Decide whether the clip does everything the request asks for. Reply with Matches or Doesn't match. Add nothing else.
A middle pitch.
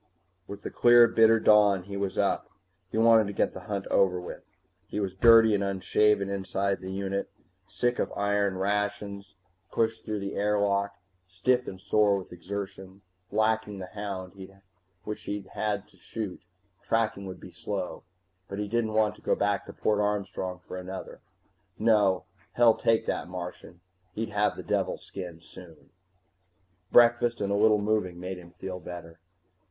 Doesn't match